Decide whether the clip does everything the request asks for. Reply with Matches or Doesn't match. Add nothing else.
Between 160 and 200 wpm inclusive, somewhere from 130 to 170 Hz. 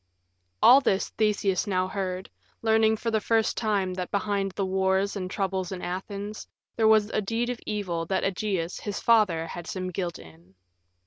Doesn't match